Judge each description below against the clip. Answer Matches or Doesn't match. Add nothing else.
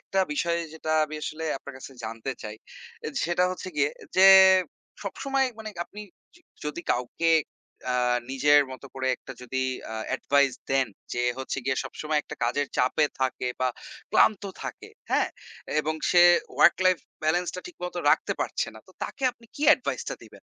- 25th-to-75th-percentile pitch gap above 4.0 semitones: Matches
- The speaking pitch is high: Doesn't match